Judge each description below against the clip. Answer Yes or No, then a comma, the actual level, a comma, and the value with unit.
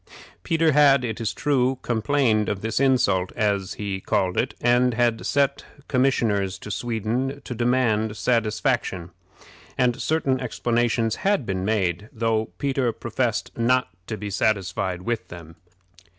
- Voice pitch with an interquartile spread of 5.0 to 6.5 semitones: No, average, 3.7 semitones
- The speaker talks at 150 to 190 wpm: No, slow, 135 wpm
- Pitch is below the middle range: Yes, low, 115 Hz